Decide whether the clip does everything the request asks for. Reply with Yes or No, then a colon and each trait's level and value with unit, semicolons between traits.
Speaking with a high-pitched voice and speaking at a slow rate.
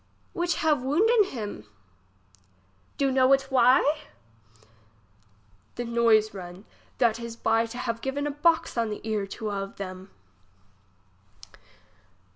Yes: high, 235 Hz; slow, 125 wpm